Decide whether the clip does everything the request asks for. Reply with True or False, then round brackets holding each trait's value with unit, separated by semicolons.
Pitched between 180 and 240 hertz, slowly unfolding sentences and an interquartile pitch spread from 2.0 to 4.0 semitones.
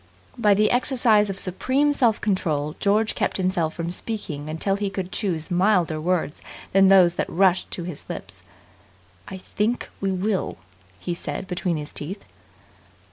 False (190 Hz; 155 wpm; 3.5 semitones)